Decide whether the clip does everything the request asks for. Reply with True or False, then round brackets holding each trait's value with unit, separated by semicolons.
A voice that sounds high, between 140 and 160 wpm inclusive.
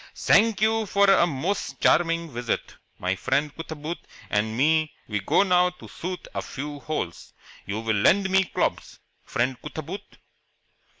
False (160 Hz; 145 wpm)